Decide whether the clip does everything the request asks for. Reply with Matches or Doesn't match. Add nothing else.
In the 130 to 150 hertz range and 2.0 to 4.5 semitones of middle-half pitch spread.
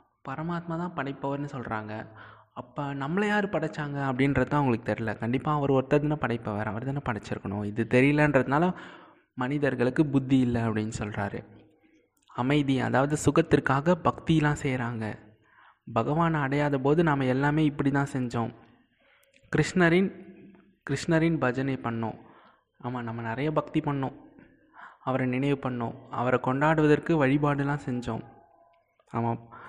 Matches